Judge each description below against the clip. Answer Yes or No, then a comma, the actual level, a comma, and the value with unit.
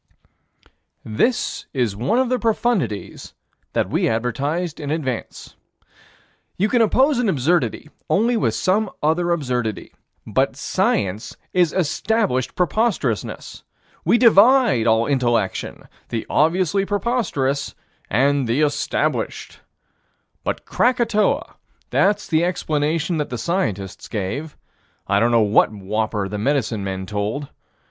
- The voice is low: No, medium, 150 Hz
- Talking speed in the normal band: No, slow, 115 wpm